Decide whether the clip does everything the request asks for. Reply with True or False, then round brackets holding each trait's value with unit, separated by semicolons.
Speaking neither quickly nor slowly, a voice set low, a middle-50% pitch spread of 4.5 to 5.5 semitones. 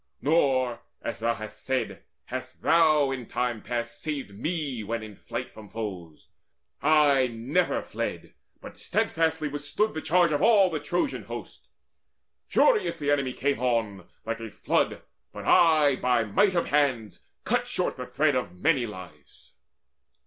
True (150 wpm; 130 Hz; 5.2 semitones)